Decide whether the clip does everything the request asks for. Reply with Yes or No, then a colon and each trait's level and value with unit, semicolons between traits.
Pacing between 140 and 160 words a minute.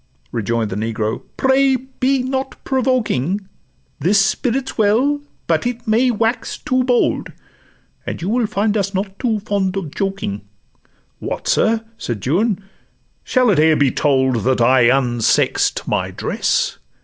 Yes: average, 145 wpm